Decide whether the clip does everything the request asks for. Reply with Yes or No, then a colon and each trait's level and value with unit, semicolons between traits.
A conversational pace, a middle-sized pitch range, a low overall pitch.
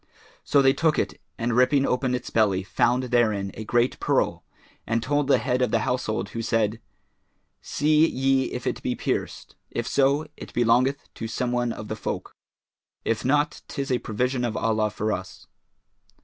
Yes: average, 175 wpm; average, 3.2 semitones; low, 120 Hz